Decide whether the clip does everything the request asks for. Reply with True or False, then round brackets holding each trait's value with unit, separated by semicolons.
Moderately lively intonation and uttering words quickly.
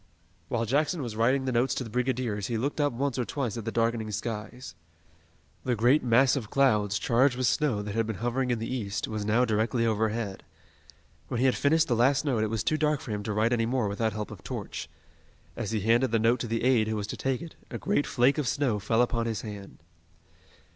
True (3.1 semitones; 235 wpm)